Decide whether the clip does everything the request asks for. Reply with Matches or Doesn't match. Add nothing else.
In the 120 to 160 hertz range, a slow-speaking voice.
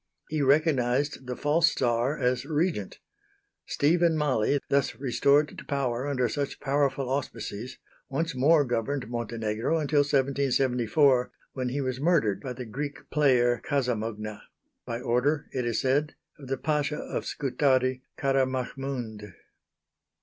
Matches